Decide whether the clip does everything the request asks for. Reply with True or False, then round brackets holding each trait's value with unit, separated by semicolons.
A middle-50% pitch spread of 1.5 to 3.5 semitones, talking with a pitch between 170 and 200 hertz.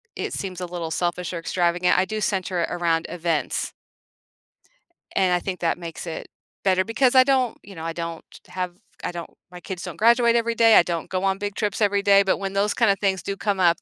True (2.8 semitones; 185 Hz)